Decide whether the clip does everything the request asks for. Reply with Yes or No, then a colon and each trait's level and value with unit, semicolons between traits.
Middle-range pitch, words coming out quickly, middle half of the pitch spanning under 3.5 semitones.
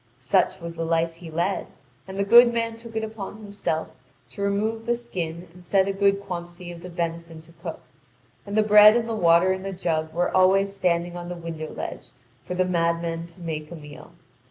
Yes: medium, 180 Hz; fast, 210 wpm; average, 3.1 semitones